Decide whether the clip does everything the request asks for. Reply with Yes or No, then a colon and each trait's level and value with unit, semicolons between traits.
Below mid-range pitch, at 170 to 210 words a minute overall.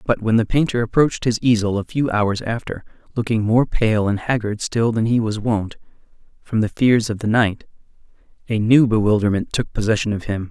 Yes: low, 110 Hz; average, 195 wpm